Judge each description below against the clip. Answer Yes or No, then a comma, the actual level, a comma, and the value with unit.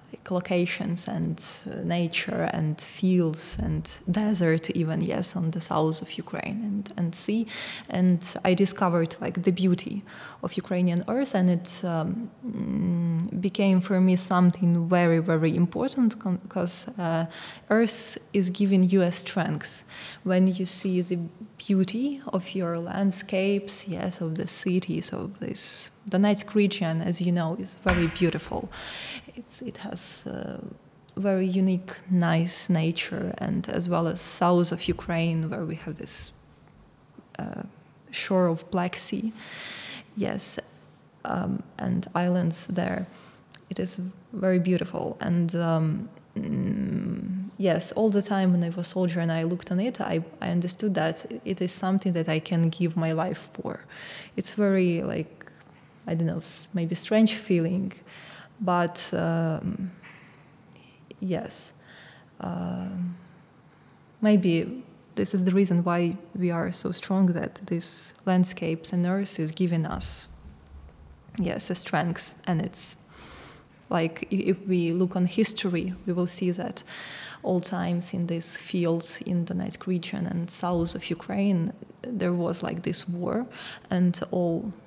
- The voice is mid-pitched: Yes, medium, 180 Hz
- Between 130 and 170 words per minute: Yes, average, 140 wpm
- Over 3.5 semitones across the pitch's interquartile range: No, narrow, 2.4 semitones